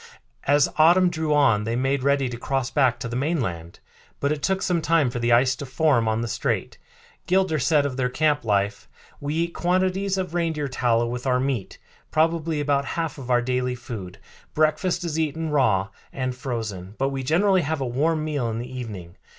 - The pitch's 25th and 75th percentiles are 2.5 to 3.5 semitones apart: No, average, 4.7 semitones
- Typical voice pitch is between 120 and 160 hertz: Yes, low, 135 Hz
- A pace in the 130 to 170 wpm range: No, average, 200 wpm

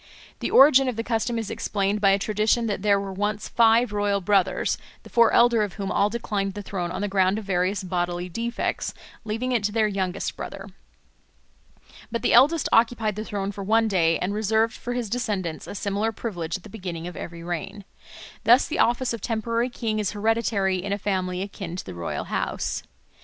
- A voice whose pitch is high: Yes, high, 205 Hz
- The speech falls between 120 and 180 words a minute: No, average, 200 wpm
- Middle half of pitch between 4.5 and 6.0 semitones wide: No, average, 3.0 semitones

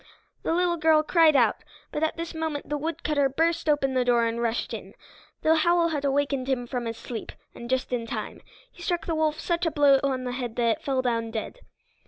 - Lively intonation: No, average, 4.6 semitones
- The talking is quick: Yes, fast, 225 wpm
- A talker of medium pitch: No, very high, 280 Hz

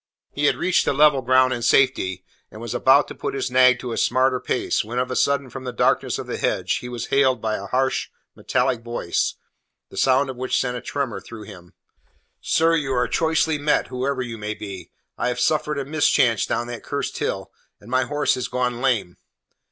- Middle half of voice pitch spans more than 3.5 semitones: No, narrow, 2.5 semitones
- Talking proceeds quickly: Yes, fast, 215 wpm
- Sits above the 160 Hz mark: No, low, 125 Hz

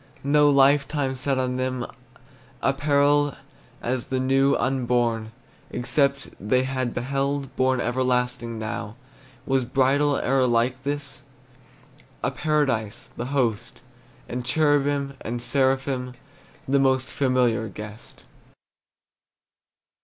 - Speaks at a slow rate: Yes, slow, 100 wpm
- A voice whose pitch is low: Yes, low, 130 Hz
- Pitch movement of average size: No, narrow, 2.2 semitones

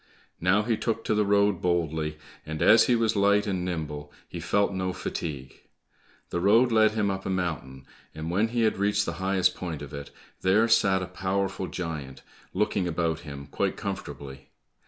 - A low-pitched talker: Yes, very low, 95 Hz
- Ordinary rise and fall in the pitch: Yes, average, 4.5 semitones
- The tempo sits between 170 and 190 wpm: Yes, average, 180 wpm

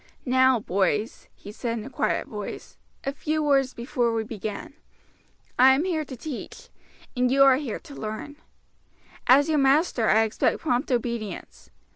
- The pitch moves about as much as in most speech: Yes, average, 3.9 semitones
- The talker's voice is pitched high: Yes, very high, 255 Hz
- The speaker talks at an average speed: Yes, average, 160 wpm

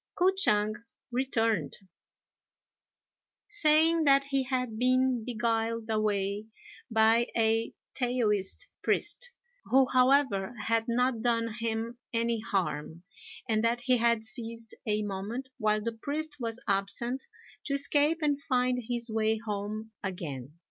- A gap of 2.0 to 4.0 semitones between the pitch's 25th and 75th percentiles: Yes, average, 3.0 semitones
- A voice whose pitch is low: No, high, 230 Hz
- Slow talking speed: Yes, slow, 120 wpm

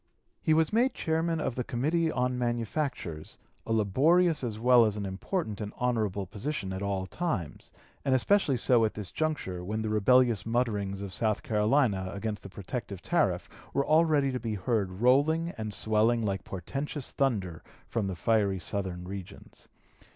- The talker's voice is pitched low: Yes, low, 115 Hz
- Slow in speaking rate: No, average, 165 wpm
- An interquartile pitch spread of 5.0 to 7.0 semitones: Yes, wide, 5.6 semitones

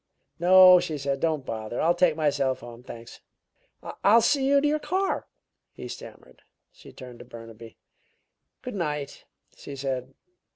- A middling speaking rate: Yes, average, 150 wpm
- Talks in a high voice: No, medium, 150 Hz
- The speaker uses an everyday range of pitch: No, wide, 6.6 semitones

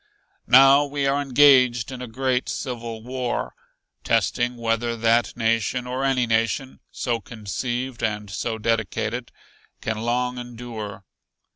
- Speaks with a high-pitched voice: No, low, 120 Hz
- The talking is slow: Yes, slow, 125 wpm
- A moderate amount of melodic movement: No, narrow, 2.2 semitones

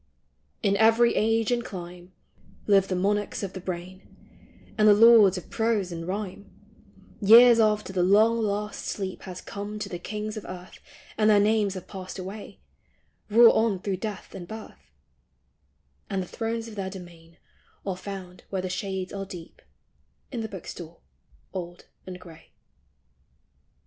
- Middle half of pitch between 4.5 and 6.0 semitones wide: No, average, 2.8 semitones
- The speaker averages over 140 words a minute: Yes, average, 160 wpm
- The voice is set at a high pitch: Yes, high, 195 Hz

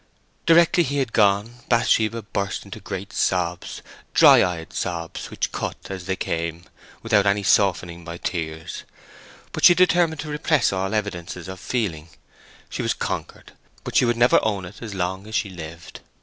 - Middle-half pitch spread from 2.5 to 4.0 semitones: No, average, 5.0 semitones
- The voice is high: No, low, 100 Hz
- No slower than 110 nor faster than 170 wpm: Yes, average, 165 wpm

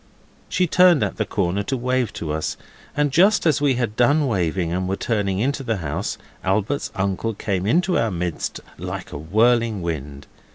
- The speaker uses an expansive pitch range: Yes, wide, 6.4 semitones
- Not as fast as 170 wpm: No, average, 180 wpm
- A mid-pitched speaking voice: No, low, 110 Hz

